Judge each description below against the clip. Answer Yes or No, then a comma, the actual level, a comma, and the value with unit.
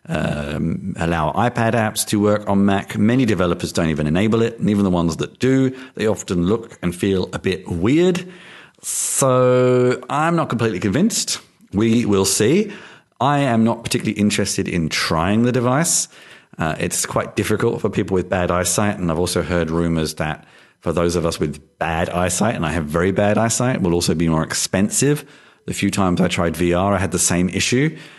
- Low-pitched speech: Yes, low, 100 Hz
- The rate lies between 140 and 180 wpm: No, average, 190 wpm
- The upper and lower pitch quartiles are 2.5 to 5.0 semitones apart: No, wide, 5.5 semitones